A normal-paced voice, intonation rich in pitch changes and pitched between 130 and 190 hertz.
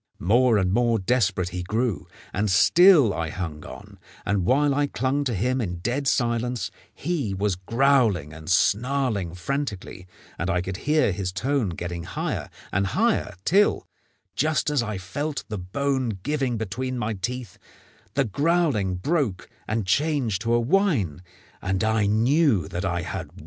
No: average, 160 wpm; wide, 6.7 semitones; low, 115 Hz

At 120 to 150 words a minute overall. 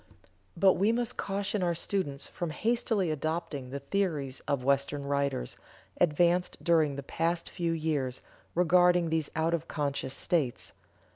Yes: average, 145 wpm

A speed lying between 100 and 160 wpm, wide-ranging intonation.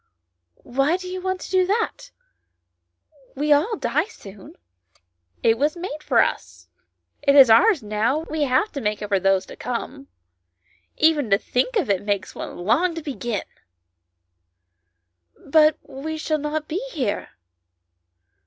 Yes: average, 155 wpm; wide, 7.8 semitones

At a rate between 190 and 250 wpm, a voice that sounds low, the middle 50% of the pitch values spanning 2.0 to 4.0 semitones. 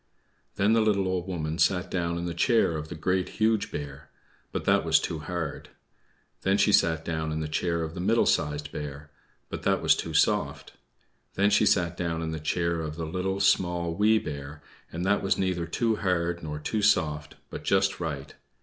Yes: average, 200 wpm; very low, 85 Hz; average, 3.5 semitones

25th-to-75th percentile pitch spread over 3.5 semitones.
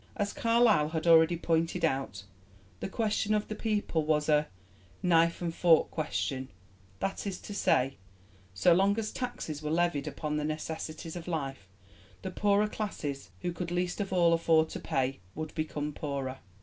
Yes: average, 4.1 semitones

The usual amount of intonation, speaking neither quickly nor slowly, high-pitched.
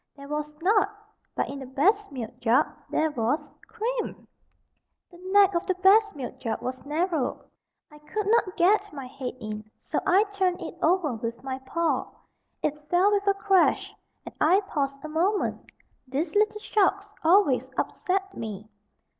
No: wide, 6.6 semitones; average, 165 wpm; very high, 335 Hz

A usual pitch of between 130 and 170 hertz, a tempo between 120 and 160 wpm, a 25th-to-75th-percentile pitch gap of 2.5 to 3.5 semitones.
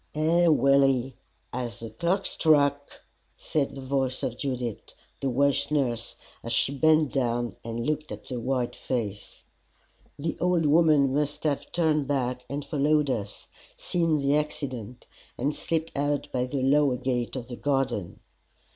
Yes: medium, 140 Hz; average, 150 wpm; average, 3.2 semitones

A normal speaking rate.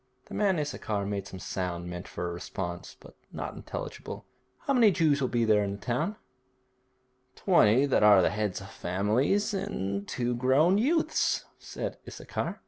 Yes: average, 160 wpm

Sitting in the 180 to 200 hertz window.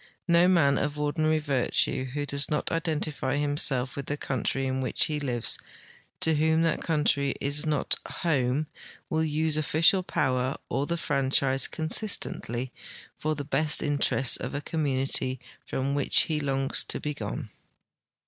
No: medium, 145 Hz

